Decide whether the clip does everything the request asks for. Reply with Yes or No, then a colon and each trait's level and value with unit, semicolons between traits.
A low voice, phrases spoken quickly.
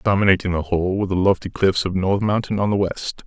Yes: very low, 95 Hz; fast, 240 wpm